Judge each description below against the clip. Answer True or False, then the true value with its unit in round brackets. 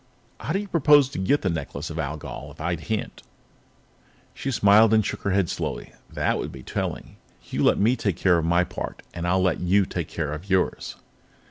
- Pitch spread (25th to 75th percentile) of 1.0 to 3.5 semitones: False (4.7 semitones)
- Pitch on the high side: False (95 Hz)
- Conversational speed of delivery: False (210 wpm)